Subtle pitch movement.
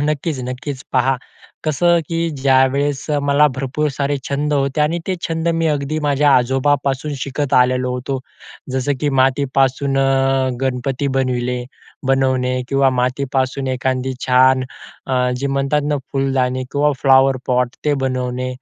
Yes: narrow, 1.9 semitones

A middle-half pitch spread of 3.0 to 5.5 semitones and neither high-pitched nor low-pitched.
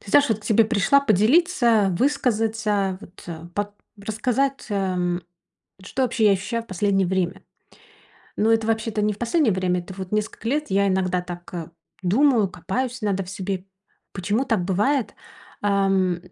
No: average, 3.5 semitones; high, 205 Hz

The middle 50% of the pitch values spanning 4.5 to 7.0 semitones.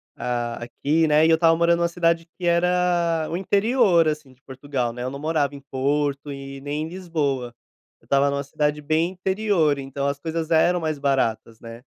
No: average, 3.5 semitones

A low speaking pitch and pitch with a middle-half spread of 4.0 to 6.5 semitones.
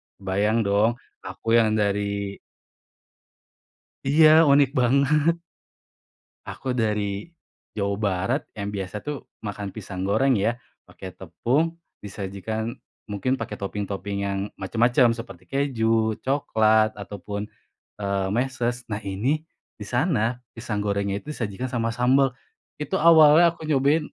Yes: low, 110 Hz; average, 4.4 semitones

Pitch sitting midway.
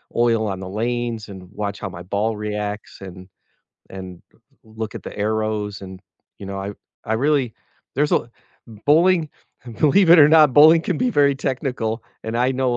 No: low, 110 Hz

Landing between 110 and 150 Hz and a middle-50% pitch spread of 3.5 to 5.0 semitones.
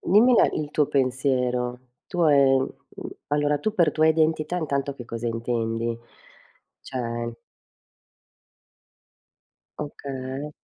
Yes: low, 135 Hz; average, 3.8 semitones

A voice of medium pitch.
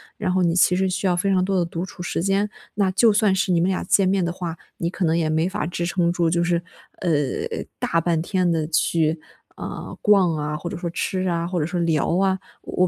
Yes: medium, 175 Hz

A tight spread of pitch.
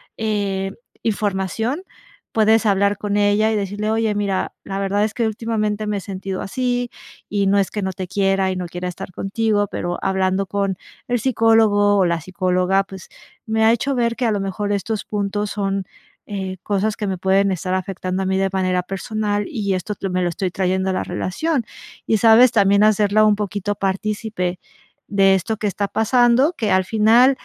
Yes: narrow, 2.2 semitones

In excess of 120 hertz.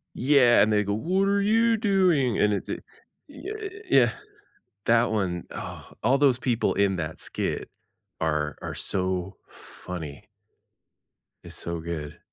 No: low, 110 Hz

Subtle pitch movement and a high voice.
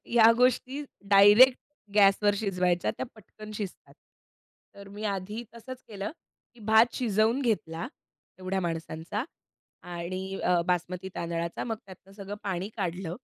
No: average, 3.4 semitones; high, 195 Hz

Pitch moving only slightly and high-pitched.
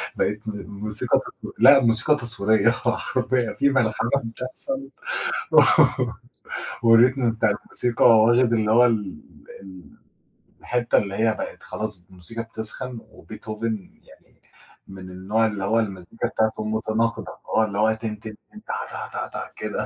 No: narrow, 2.0 semitones; low, 110 Hz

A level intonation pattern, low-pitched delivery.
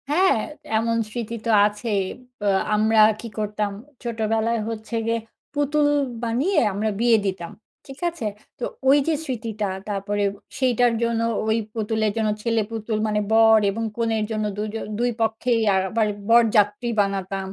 No: narrow, 1.9 semitones; high, 225 Hz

